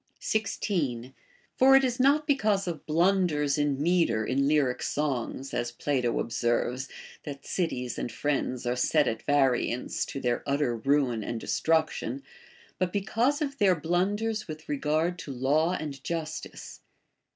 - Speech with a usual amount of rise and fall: No, wide, 6.1 semitones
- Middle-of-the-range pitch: Yes, medium, 150 Hz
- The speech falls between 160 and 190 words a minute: No, average, 145 wpm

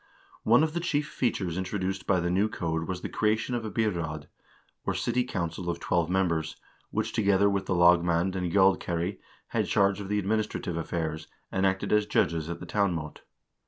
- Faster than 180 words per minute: Yes, average, 190 wpm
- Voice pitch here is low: Yes, very low, 95 Hz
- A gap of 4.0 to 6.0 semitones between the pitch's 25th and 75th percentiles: No, average, 3.5 semitones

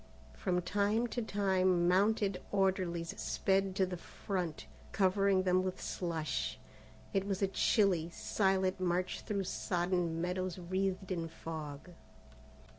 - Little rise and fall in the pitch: Yes, narrow, 1.8 semitones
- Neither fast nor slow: No, slow, 120 wpm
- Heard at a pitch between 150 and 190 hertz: Yes, medium, 185 Hz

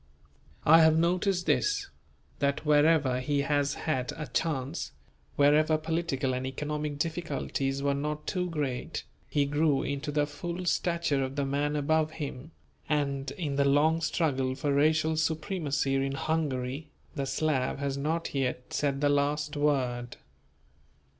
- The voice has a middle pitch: Yes, medium, 145 Hz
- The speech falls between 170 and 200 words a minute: No, average, 140 wpm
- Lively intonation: No, narrow, 2.4 semitones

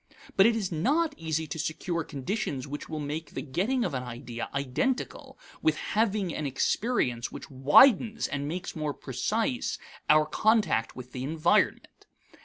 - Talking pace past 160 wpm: No, average, 155 wpm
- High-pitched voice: No, medium, 160 Hz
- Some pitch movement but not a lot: No, wide, 7.5 semitones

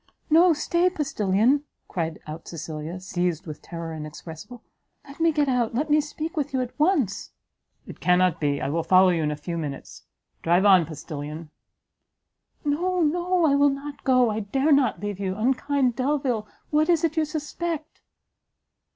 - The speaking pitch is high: Yes, high, 245 Hz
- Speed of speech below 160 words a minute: No, average, 170 wpm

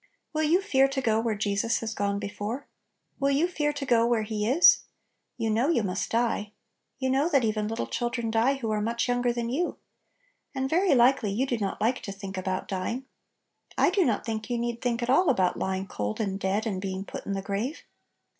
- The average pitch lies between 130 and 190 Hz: No, high, 230 Hz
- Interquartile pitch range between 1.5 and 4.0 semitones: No, average, 4.4 semitones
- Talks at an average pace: No, fast, 220 wpm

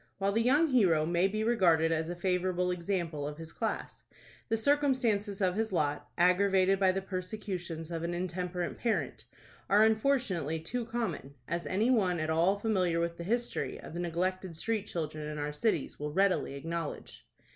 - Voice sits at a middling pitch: Yes, medium, 180 Hz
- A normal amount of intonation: Yes, average, 4.2 semitones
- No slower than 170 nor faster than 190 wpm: Yes, average, 175 wpm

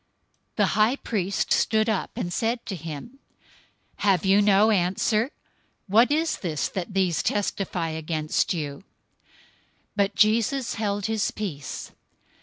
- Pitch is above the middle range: Yes, high, 200 Hz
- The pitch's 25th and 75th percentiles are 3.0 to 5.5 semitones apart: Yes, average, 3.9 semitones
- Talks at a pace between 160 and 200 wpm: No, average, 140 wpm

